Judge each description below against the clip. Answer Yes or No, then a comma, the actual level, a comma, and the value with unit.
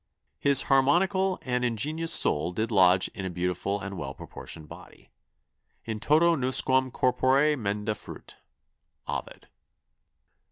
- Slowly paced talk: Yes, slow, 120 wpm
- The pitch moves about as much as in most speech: No, wide, 6.4 semitones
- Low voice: Yes, low, 125 Hz